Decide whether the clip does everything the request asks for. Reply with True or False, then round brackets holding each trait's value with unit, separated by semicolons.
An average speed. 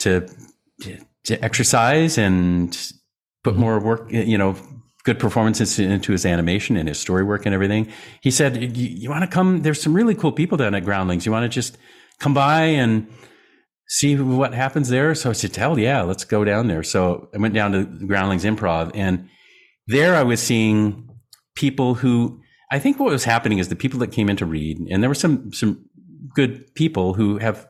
True (195 wpm)